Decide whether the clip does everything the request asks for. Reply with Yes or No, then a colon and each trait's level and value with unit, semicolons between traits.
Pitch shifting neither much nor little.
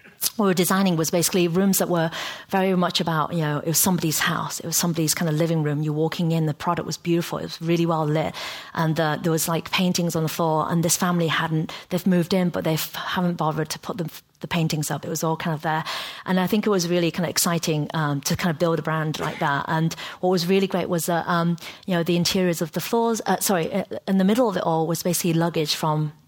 No: narrow, 2.0 semitones